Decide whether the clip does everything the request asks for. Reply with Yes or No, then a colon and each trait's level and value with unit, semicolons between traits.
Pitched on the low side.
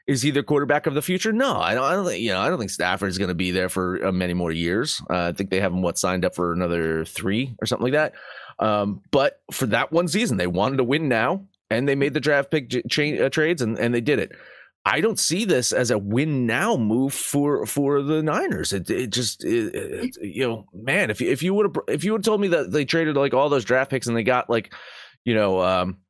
Yes: low, 130 Hz